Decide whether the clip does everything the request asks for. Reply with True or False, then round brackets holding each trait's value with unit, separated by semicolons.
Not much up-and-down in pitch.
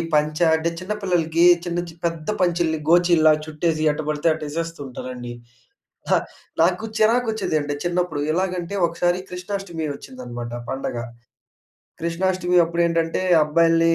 True (2.3 semitones)